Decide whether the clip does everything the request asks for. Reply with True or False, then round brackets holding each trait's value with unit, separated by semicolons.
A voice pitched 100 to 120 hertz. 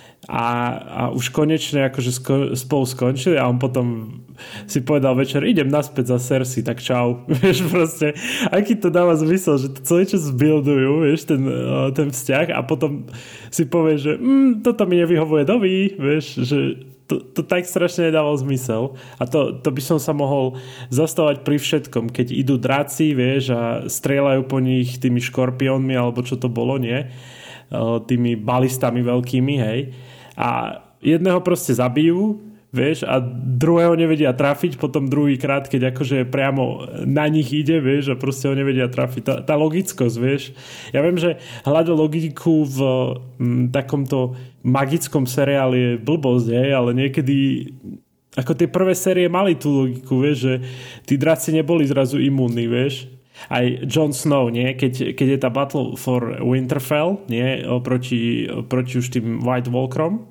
False (135 Hz)